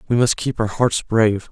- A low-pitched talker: Yes, low, 110 Hz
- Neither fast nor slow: No, fast, 240 wpm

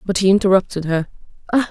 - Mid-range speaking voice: No, high, 195 Hz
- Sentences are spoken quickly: No, average, 140 wpm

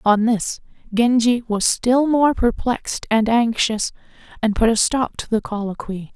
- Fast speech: No, average, 155 wpm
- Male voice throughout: No, female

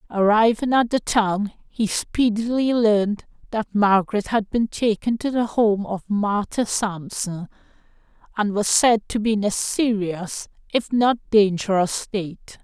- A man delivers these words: No, female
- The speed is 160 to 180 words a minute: No, average, 145 wpm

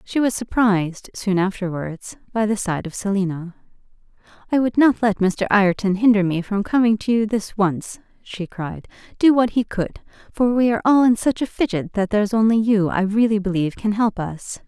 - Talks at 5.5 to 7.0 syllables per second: No, 5.3 syllables/s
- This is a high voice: Yes, high, 210 Hz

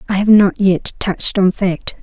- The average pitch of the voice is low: No, high, 195 Hz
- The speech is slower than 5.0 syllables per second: Yes, 4.5 syllables/s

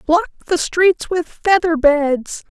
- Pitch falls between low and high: No, very high, 335 Hz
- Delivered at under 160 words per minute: Yes, average, 140 wpm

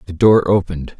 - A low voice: Yes, very low, 90 Hz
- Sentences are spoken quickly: No, average, 180 wpm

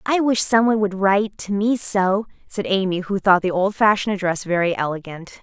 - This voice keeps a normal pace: Yes, average, 190 wpm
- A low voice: No, high, 195 Hz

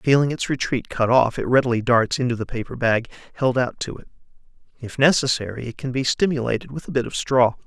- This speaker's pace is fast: Yes, fast, 210 wpm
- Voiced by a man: Yes, male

